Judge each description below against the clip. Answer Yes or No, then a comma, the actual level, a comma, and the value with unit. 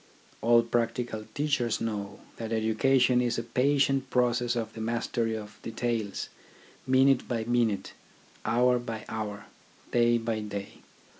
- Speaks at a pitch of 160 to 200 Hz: No, low, 115 Hz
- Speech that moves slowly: Yes, slow, 130 wpm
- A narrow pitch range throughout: Yes, narrow, 1.8 semitones